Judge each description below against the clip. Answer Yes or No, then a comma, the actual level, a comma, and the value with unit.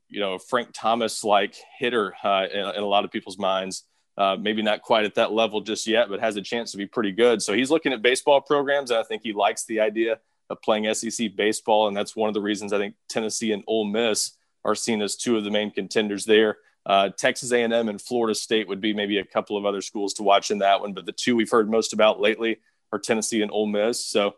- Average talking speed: No, fast, 250 wpm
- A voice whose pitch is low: Yes, low, 110 Hz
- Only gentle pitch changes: Yes, narrow, 1.9 semitones